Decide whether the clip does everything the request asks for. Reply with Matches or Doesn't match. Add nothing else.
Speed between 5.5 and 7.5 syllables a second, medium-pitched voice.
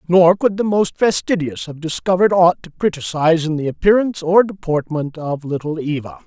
Matches